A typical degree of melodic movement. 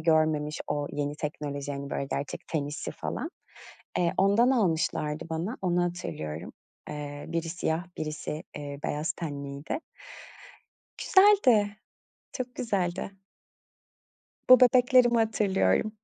No: wide, 6.1 semitones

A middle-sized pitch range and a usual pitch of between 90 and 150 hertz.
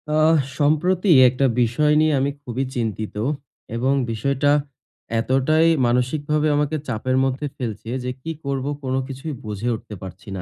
Yes: average, 3.9 semitones; low, 135 Hz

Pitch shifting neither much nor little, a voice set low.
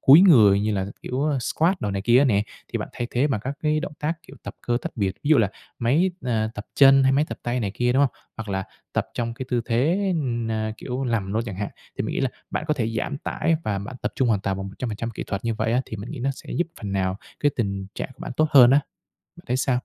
Yes: average, 4.4 semitones; low, 120 Hz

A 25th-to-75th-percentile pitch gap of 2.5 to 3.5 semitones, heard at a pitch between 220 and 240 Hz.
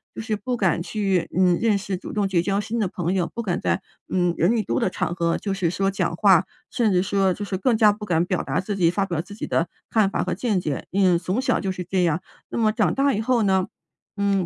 No: average, 2.9 semitones; high, 195 Hz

